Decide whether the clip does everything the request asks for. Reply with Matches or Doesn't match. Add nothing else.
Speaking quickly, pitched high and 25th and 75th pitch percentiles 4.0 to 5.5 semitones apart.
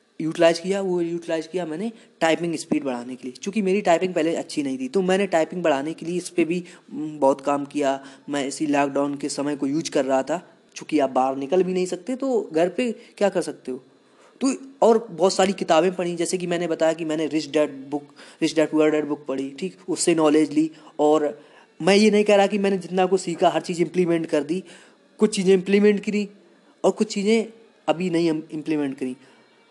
Doesn't match